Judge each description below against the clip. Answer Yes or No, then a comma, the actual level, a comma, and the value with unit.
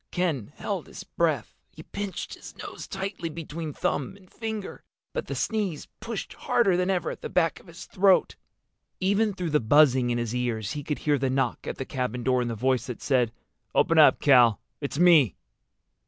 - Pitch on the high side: No, medium, 150 Hz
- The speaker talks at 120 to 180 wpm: No, average, 195 wpm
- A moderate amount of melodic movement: No, wide, 6.6 semitones